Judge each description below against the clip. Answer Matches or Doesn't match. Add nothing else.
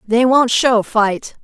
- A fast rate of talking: Doesn't match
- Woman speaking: Matches